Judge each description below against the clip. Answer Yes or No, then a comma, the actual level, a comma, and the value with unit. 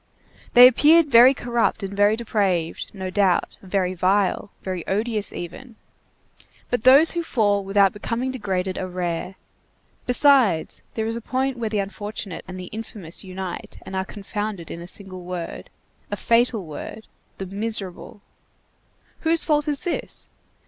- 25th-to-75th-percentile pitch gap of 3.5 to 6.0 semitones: Yes, average, 4.2 semitones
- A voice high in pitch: Yes, high, 205 Hz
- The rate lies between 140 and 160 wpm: Yes, average, 150 wpm